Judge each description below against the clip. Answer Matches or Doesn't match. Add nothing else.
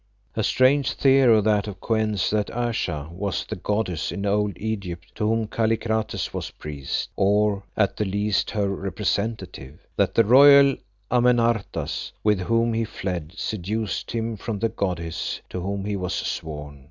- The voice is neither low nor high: Doesn't match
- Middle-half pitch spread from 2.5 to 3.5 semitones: Matches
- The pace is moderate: Matches